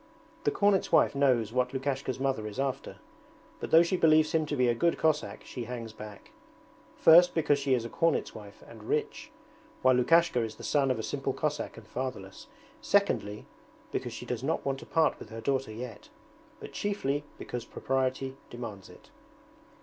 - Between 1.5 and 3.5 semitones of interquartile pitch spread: No, average, 4.5 semitones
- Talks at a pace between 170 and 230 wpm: Yes, average, 180 wpm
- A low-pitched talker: Yes, low, 130 Hz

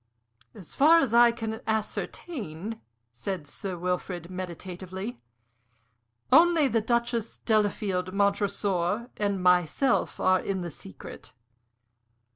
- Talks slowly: Yes, slow, 100 wpm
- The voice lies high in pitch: Yes, high, 200 Hz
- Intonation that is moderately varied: Yes, average, 4.2 semitones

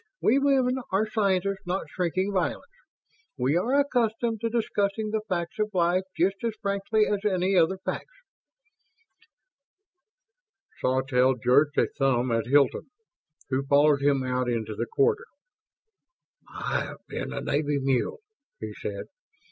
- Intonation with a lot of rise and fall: Yes, wide, 7.9 semitones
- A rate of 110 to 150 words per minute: Yes, slow, 135 wpm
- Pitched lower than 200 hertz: Yes, medium, 185 Hz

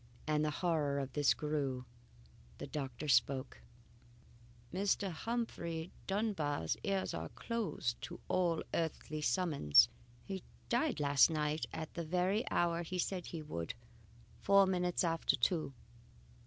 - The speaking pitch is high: No, medium, 165 Hz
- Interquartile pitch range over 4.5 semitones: No, average, 4.2 semitones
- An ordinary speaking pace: No, slow, 130 wpm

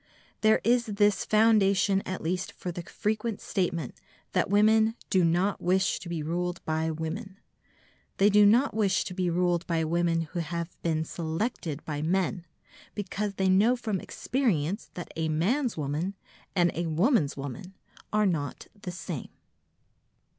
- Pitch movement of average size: Yes, average, 4.0 semitones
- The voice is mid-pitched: Yes, medium, 180 Hz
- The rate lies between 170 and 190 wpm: No, average, 155 wpm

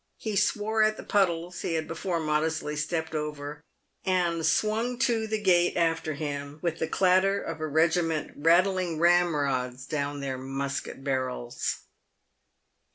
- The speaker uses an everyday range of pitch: Yes, average, 3.9 semitones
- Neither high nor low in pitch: Yes, medium, 165 Hz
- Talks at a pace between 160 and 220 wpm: No, average, 140 wpm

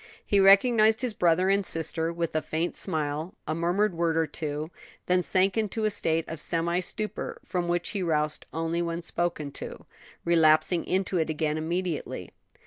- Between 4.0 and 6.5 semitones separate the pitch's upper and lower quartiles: No, average, 2.7 semitones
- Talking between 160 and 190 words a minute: Yes, average, 170 wpm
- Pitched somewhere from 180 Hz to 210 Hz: No, medium, 170 Hz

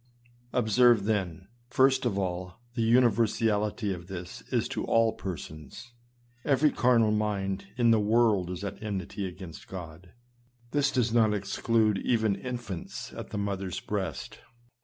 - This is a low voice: Yes, low, 105 Hz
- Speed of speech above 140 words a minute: No, slow, 135 wpm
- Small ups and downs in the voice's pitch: No, average, 3.6 semitones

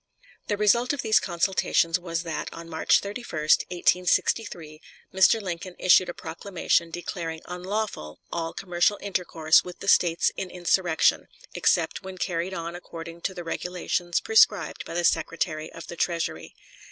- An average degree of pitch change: No, narrow, 2.2 semitones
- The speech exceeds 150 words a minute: No, average, 145 wpm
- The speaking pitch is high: No, medium, 175 Hz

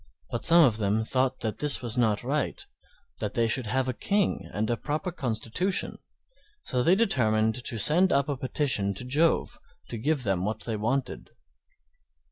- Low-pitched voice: Yes, low, 125 Hz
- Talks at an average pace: Yes, average, 175 wpm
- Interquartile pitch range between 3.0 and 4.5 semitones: No, average, 5.1 semitones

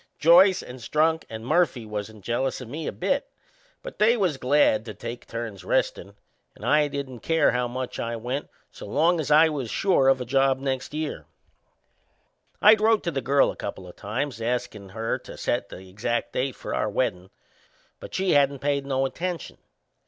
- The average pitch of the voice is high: No, low, 135 Hz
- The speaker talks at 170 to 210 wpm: Yes, average, 190 wpm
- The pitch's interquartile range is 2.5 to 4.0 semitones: No, average, 5.1 semitones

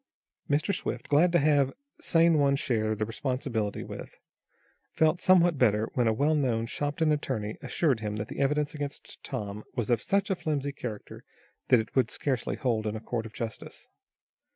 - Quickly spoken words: No, average, 175 wpm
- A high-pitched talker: No, low, 130 Hz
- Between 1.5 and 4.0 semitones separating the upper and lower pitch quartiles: No, average, 5.1 semitones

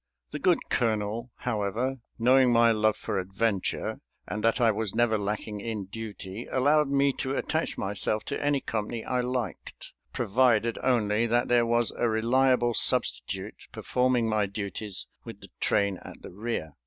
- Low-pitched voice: Yes, low, 115 Hz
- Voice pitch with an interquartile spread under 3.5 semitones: Yes, average, 3.0 semitones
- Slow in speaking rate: No, average, 155 wpm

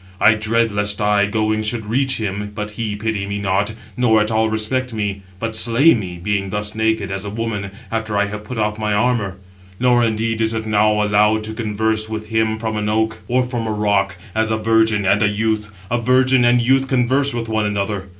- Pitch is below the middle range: Yes, low, 110 Hz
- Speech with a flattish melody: Yes, narrow, 1.6 semitones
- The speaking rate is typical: No, fast, 215 wpm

